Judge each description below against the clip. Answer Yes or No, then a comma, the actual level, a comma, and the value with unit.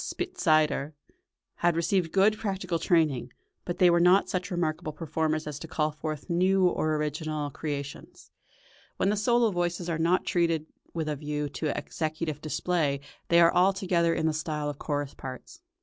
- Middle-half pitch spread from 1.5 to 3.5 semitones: Yes, average, 2.8 semitones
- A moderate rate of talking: Yes, average, 165 wpm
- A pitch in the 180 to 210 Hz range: No, medium, 165 Hz